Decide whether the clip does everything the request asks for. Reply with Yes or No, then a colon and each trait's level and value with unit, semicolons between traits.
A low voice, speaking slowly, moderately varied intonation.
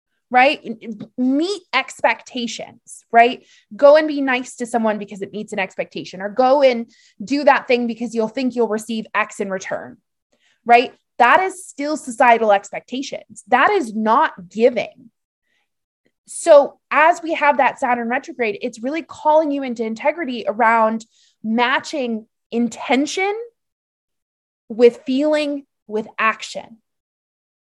No: high, 245 Hz; slow, 130 wpm; average, 4.3 semitones